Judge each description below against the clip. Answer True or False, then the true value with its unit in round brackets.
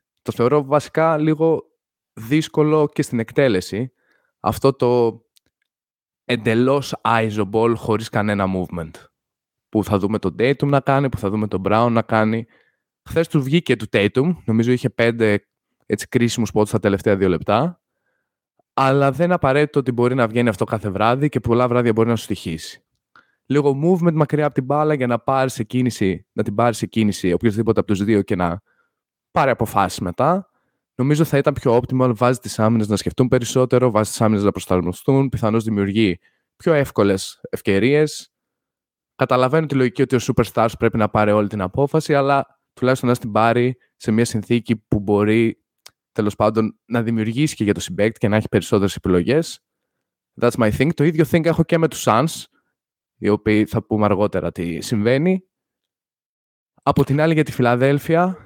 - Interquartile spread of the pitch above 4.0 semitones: True (4.4 semitones)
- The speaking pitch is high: False (120 Hz)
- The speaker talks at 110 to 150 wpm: False (170 wpm)